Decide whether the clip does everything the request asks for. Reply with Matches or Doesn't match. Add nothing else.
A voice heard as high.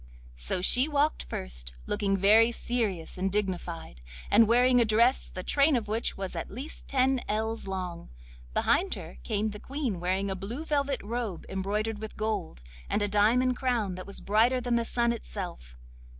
Matches